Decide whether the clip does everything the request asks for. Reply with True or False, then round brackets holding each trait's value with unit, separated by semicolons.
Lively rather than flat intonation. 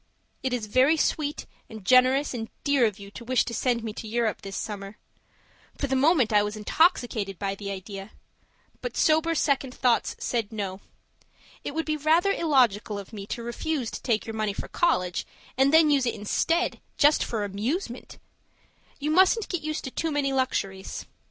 True (6.1 semitones)